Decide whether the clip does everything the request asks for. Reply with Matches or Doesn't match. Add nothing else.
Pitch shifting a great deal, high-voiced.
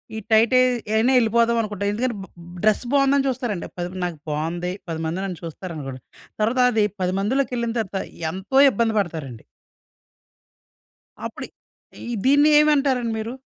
Matches